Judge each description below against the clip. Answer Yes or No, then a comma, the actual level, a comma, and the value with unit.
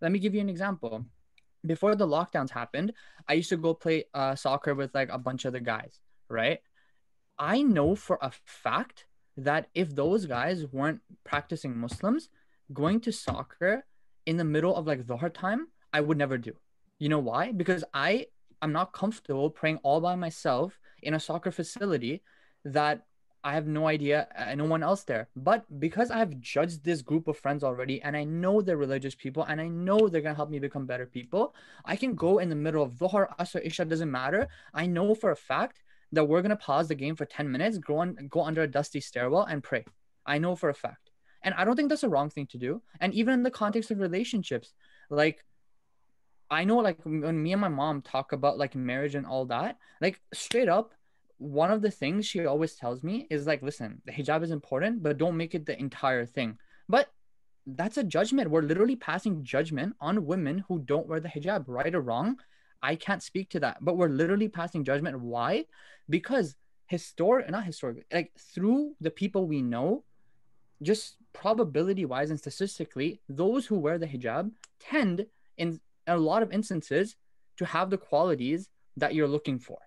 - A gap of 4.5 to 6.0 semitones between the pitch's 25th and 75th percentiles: Yes, average, 5.1 semitones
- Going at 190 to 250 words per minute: Yes, average, 200 wpm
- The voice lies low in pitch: No, medium, 160 Hz